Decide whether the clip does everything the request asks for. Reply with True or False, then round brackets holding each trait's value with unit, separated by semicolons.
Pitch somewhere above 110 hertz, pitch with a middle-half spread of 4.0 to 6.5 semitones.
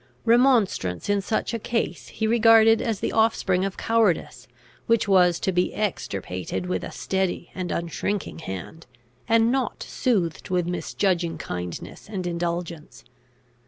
True (190 Hz; 4.8 semitones)